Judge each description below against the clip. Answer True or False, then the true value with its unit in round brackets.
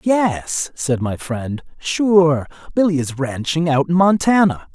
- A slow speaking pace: True (125 wpm)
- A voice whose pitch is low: False (160 Hz)